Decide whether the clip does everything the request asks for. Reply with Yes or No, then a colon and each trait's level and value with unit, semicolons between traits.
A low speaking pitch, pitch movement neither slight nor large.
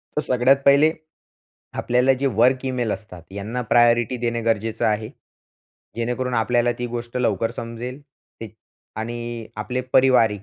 No: low, 120 Hz; narrow, 1.9 semitones